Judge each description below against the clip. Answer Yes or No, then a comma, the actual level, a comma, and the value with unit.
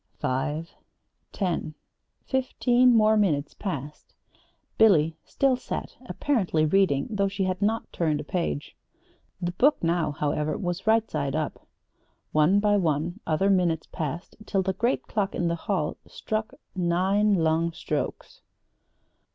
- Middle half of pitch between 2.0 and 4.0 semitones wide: No, average, 4.8 semitones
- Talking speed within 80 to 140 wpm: Yes, slow, 135 wpm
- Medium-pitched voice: Yes, medium, 180 Hz